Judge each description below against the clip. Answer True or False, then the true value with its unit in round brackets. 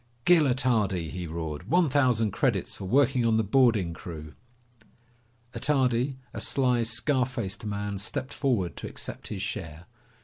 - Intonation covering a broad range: True (5.7 semitones)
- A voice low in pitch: True (115 Hz)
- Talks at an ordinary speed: True (145 wpm)